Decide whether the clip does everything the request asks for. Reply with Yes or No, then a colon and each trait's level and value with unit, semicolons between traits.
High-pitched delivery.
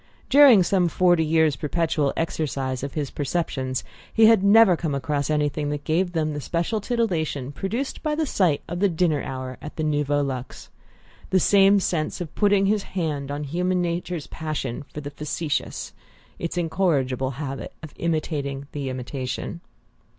No: medium, 155 Hz